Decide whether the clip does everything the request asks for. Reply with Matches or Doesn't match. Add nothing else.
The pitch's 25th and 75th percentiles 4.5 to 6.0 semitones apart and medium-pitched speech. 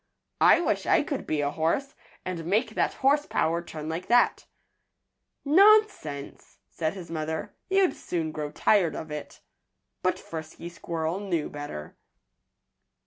Matches